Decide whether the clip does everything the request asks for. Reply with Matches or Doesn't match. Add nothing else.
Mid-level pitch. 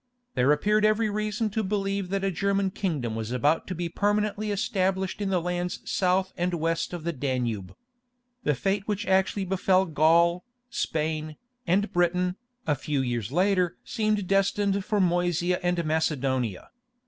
Matches